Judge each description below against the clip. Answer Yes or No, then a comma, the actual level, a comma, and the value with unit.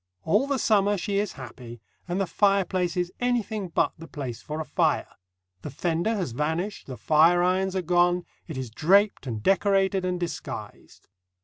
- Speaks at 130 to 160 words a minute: No, average, 170 wpm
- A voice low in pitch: No, medium, 180 Hz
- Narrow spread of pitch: No, average, 3.9 semitones